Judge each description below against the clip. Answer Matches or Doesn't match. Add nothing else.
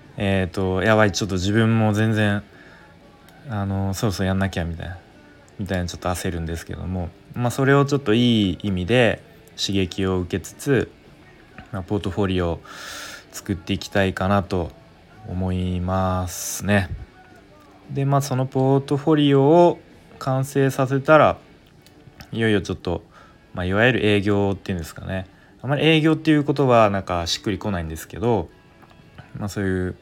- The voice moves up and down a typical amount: Matches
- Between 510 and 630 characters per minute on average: Doesn't match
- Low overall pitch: Matches